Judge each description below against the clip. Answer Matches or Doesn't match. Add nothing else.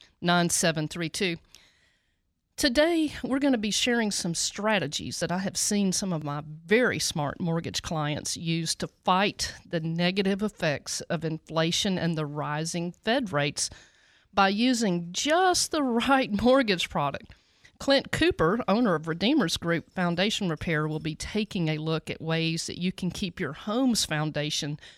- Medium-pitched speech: Matches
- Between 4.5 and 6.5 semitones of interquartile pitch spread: Matches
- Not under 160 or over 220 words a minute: Doesn't match